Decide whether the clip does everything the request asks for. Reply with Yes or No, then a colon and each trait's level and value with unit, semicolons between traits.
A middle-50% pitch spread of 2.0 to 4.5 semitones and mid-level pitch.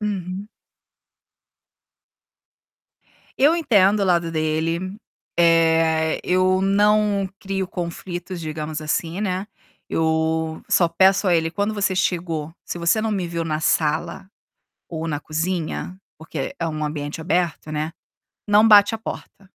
Yes: average, 3.4 semitones; medium, 170 Hz